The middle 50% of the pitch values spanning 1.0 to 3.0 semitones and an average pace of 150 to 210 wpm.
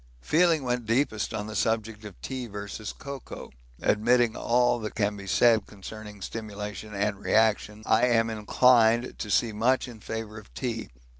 Yes: narrow, 2.4 semitones; average, 160 wpm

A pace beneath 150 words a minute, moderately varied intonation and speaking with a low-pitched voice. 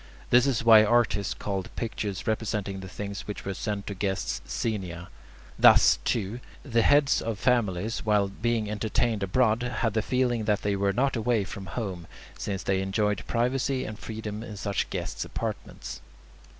No: average, 165 wpm; average, 3.0 semitones; low, 105 Hz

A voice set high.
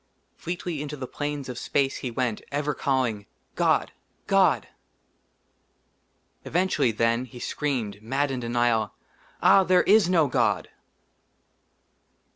No: low, 135 Hz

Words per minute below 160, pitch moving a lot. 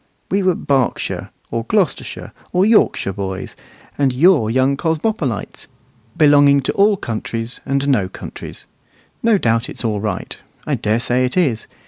Yes: average, 145 wpm; wide, 6.7 semitones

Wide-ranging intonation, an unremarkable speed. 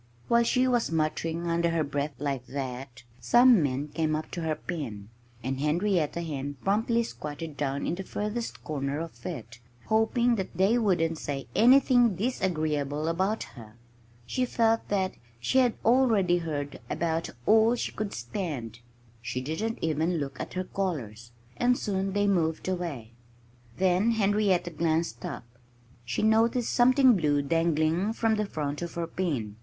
Yes: wide, 6.7 semitones; average, 150 wpm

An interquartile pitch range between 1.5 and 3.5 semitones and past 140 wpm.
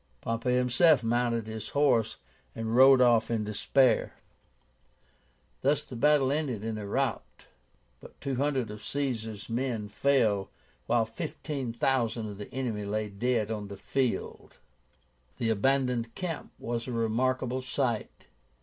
No: average, 3.2 semitones; slow, 135 wpm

